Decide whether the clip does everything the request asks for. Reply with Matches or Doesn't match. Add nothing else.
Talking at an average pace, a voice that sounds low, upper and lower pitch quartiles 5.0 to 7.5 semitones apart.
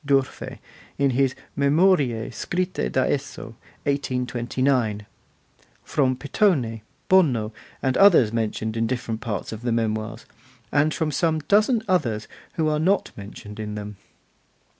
Doesn't match